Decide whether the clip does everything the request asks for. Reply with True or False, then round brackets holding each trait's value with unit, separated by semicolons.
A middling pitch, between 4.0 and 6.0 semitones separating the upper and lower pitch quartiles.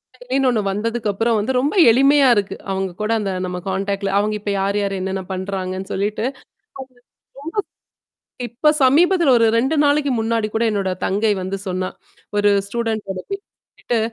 False (215 Hz; 4.3 semitones)